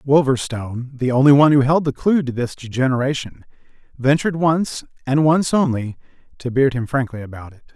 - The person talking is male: Yes, male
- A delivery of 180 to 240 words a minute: No, average, 155 wpm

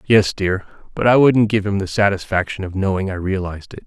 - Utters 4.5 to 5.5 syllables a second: No, 5.9 syllables/s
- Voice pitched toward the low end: Yes, low, 100 Hz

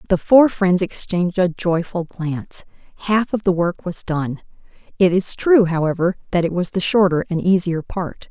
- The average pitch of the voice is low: No, medium, 180 Hz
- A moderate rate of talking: Yes, average, 180 wpm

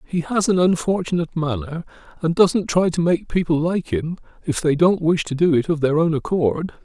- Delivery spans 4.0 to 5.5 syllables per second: Yes, 5.2 syllables/s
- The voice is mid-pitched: Yes, medium, 165 Hz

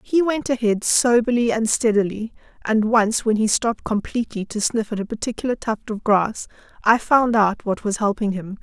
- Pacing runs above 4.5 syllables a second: Yes, 5.1 syllables/s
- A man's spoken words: No, female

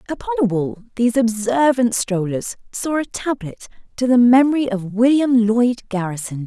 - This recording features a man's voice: No, female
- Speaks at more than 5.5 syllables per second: No, 4.8 syllables/s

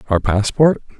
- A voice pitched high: No, low, 115 Hz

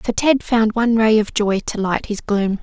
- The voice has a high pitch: Yes, high, 220 Hz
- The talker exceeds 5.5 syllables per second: No, 4.8 syllables/s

